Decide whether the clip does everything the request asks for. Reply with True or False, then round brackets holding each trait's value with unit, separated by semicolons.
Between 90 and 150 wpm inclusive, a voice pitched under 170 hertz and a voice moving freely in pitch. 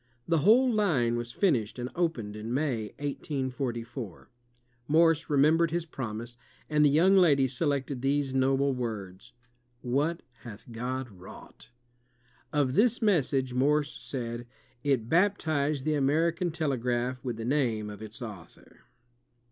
False (135 wpm; 135 Hz; 4.6 semitones)